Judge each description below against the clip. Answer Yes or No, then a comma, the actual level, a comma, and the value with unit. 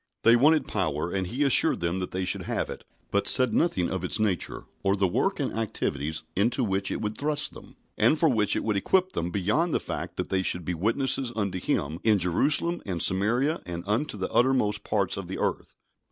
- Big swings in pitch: Yes, wide, 5.8 semitones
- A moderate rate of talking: No, fast, 215 wpm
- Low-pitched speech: Yes, low, 105 Hz